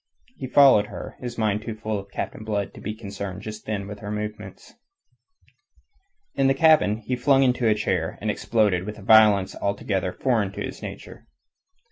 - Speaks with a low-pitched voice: Yes, low, 105 Hz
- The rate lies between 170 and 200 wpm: Yes, average, 180 wpm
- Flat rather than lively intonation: Yes, narrow, 2.3 semitones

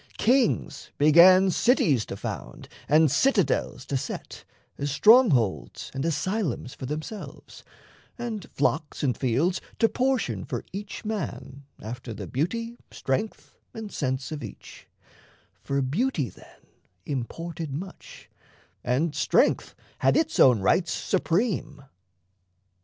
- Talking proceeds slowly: Yes, slow, 115 wpm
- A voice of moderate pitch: Yes, medium, 155 Hz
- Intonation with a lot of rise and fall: Yes, wide, 7.8 semitones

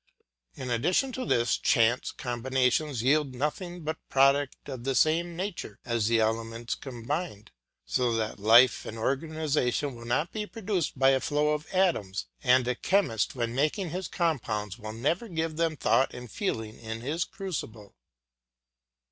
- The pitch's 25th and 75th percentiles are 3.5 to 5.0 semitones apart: No, wide, 5.6 semitones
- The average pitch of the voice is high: No, low, 135 Hz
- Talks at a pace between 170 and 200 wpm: No, average, 155 wpm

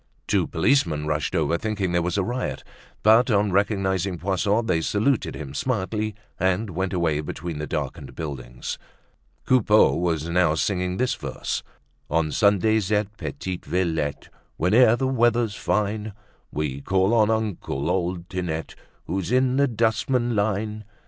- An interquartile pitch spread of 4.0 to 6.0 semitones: Yes, average, 4.5 semitones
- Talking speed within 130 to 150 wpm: Yes, average, 140 wpm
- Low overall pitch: Yes, very low, 95 Hz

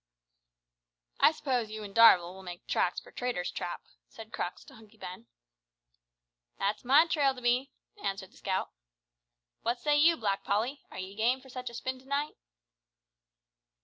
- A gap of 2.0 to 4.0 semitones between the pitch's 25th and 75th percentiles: No, average, 5.0 semitones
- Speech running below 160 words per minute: No, average, 165 wpm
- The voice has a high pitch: Yes, high, 230 Hz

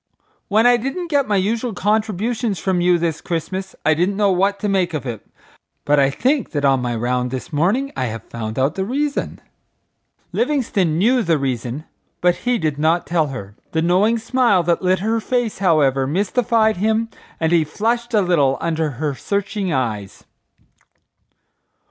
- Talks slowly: No, average, 175 wpm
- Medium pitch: Yes, medium, 180 Hz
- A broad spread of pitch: Yes, wide, 7.0 semitones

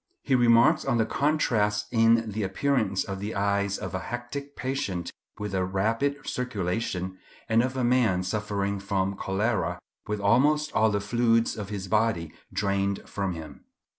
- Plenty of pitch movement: No, average, 3.6 semitones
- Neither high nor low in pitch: No, low, 105 Hz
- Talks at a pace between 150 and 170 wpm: Yes, average, 160 wpm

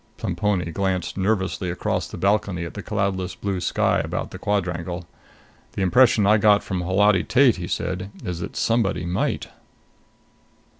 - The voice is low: Yes, very low, 95 Hz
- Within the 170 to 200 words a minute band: No, average, 150 wpm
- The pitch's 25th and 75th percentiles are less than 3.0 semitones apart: Yes, narrow, 2.6 semitones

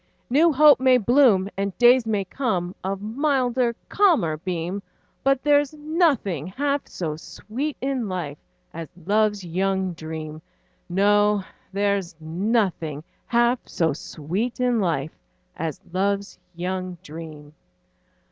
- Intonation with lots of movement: Yes, wide, 6.4 semitones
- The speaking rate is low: Yes, slow, 120 wpm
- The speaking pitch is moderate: No, high, 200 Hz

